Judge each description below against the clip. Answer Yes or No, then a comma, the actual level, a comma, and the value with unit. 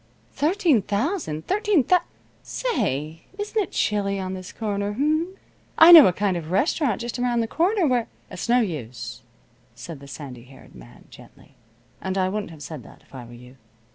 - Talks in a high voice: Yes, high, 205 Hz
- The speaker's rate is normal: Yes, average, 190 wpm